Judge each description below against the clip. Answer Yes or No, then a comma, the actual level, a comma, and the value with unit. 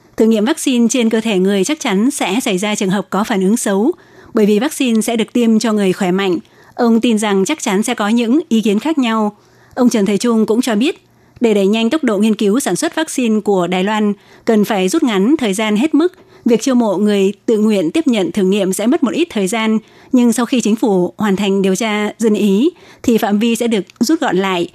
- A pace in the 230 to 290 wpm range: Yes, fast, 250 wpm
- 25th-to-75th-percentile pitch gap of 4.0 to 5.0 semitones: No, average, 3.6 semitones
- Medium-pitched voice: No, high, 220 Hz